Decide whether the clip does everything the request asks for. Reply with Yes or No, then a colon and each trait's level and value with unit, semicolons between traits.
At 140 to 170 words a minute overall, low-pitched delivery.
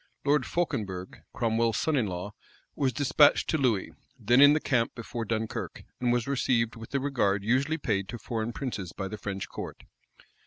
No: average, 180 wpm; low, 115 Hz